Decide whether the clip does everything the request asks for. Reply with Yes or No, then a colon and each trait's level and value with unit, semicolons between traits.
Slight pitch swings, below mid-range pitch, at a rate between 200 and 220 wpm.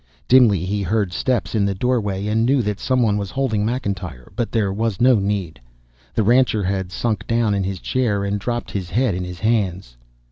No: average, 3.4 semitones; low, 105 Hz; fast, 205 wpm